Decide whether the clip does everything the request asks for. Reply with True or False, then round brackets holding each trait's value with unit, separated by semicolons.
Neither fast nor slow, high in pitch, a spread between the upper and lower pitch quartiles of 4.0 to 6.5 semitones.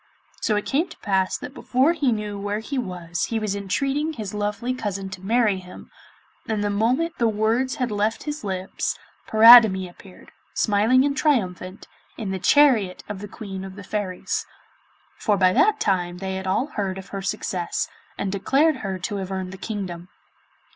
True (180 wpm; 205 Hz; 4.3 semitones)